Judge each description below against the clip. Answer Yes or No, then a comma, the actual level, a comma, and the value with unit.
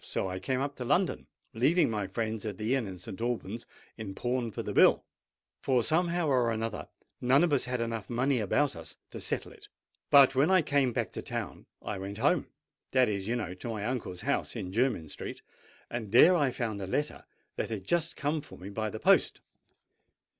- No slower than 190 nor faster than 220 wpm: Yes, fast, 205 wpm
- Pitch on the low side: Yes, low, 120 Hz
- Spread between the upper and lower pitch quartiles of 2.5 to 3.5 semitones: No, average, 5.0 semitones